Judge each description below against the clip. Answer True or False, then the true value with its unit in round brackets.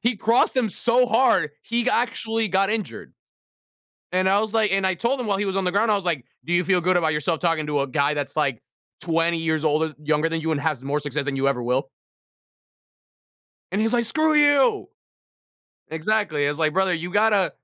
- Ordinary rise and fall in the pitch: False (6.3 semitones)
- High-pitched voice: False (180 Hz)